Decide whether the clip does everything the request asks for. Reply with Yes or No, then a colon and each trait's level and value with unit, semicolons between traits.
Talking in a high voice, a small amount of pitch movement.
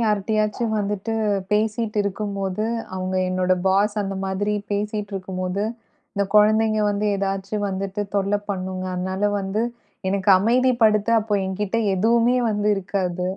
Yes: high, 205 Hz; narrow, 1.9 semitones